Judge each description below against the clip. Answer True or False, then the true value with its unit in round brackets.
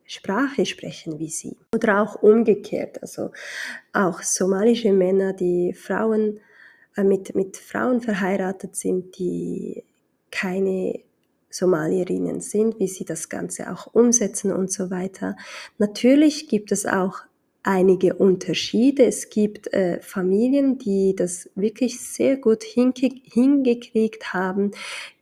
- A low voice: False (200 Hz)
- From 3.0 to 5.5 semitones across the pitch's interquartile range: True (3.5 semitones)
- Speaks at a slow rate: True (120 wpm)